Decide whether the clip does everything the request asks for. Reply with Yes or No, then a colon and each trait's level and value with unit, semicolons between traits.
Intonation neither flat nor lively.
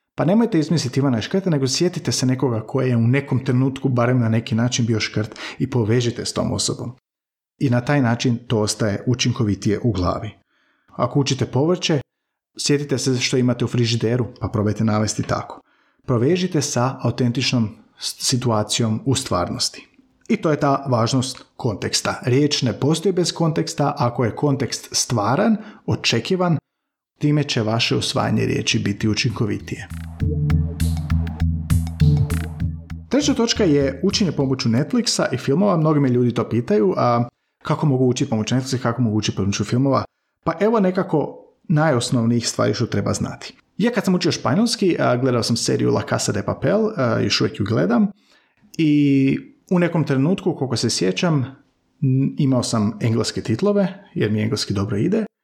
Yes: average, 5.0 semitones